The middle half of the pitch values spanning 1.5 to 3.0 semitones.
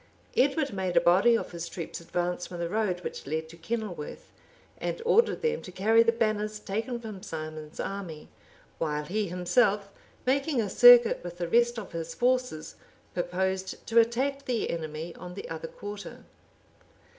No: wide, 5.5 semitones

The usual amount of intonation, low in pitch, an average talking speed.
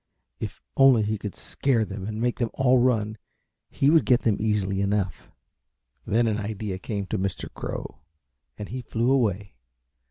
Yes: average, 3.3 semitones; low, 110 Hz; average, 165 wpm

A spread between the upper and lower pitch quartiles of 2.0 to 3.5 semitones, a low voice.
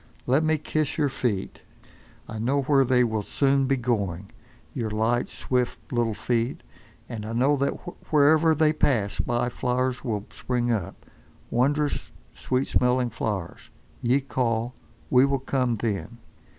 Yes: average, 3.1 semitones; low, 125 Hz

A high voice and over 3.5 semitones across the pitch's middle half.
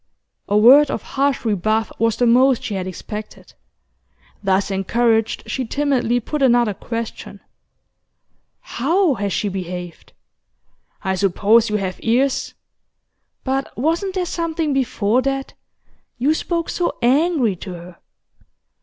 Yes: high, 235 Hz; average, 5.2 semitones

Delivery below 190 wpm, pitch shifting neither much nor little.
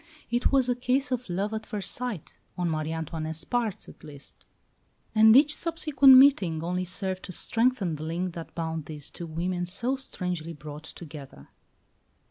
No: average, 165 wpm; wide, 7.1 semitones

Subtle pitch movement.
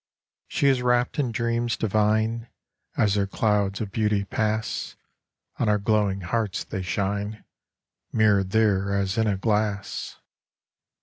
Yes: narrow, 2.0 semitones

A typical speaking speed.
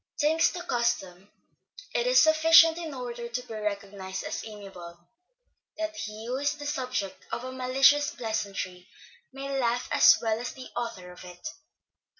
Yes: average, 155 wpm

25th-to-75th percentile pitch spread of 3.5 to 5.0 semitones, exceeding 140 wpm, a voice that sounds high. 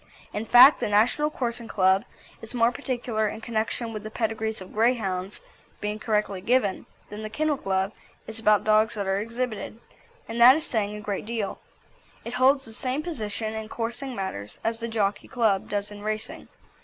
No: narrow, 2.5 semitones; average, 180 wpm; high, 220 Hz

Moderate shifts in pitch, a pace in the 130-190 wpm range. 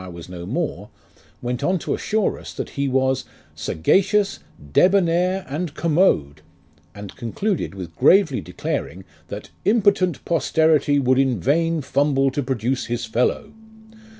No: wide, 6.9 semitones; average, 145 wpm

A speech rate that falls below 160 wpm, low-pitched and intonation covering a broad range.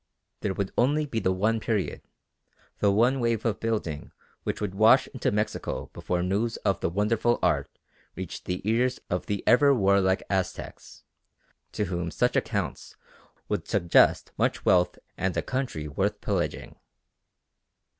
No: average, 145 wpm; low, 105 Hz; average, 3.9 semitones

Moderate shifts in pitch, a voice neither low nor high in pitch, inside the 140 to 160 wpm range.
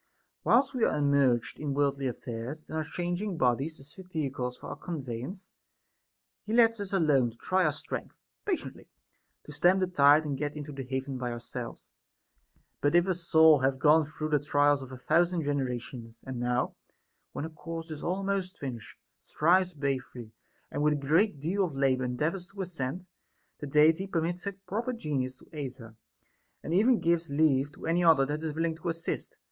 No: average, 4.4 semitones; medium, 150 Hz; average, 185 wpm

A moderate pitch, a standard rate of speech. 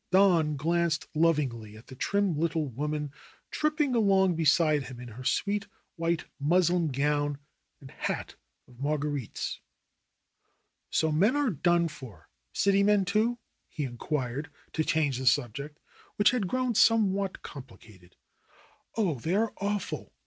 Yes: medium, 160 Hz; average, 145 wpm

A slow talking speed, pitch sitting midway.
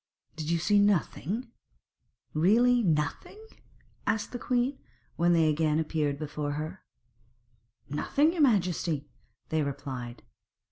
Yes: slow, 110 wpm; medium, 165 Hz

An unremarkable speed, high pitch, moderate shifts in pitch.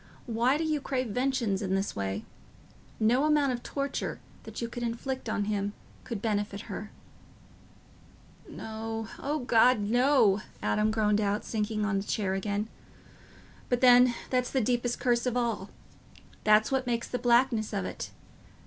Yes: average, 150 wpm; high, 230 Hz; average, 3.2 semitones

